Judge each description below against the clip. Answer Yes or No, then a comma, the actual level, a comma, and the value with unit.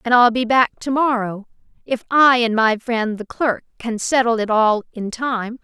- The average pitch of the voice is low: No, high, 235 Hz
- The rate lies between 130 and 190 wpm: No, average, 200 wpm